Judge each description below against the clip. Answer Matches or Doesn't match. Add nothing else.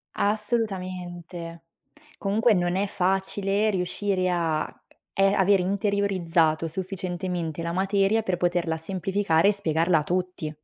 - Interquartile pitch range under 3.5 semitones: Matches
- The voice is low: Doesn't match